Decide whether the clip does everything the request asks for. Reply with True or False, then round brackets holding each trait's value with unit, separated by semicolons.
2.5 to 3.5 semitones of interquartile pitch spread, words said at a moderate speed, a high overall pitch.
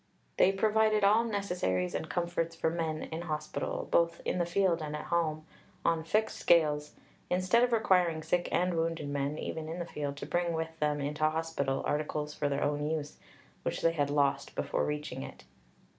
False (2.8 semitones; 185 wpm; 160 Hz)